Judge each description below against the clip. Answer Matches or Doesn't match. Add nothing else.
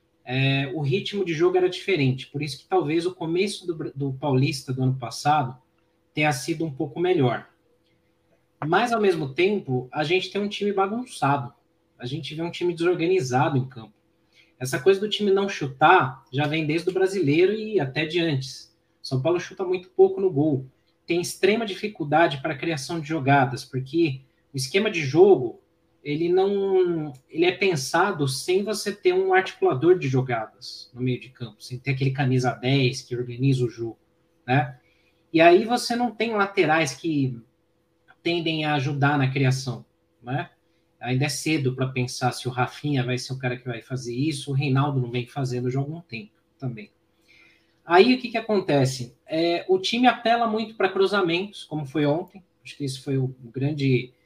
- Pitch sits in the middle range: Matches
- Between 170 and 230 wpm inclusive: Matches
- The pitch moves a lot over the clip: Matches